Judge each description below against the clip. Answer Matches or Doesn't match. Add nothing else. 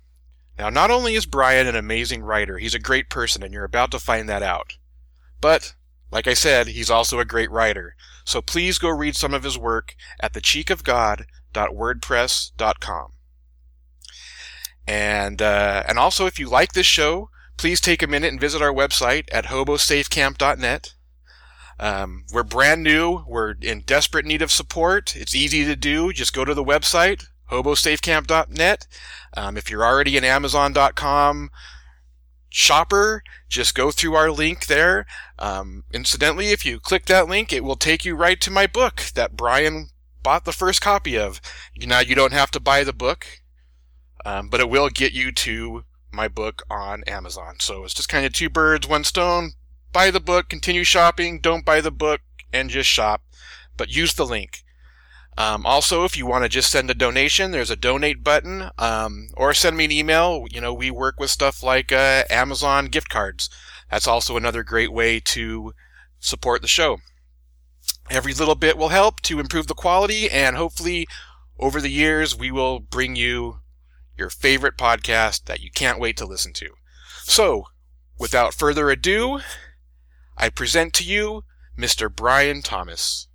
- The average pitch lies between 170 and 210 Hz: Doesn't match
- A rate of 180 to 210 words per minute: Doesn't match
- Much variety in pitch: Matches